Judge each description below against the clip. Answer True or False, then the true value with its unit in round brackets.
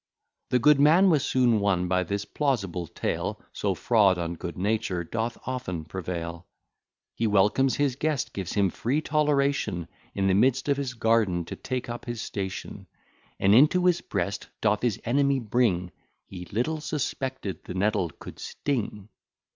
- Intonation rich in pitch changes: True (6.1 semitones)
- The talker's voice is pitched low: True (110 Hz)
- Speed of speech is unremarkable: True (160 wpm)